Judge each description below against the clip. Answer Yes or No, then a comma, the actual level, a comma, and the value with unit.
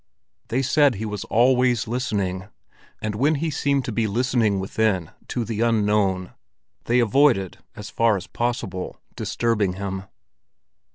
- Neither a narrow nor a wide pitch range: Yes, average, 3.8 semitones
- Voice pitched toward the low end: Yes, low, 110 Hz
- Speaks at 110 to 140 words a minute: Yes, slow, 135 wpm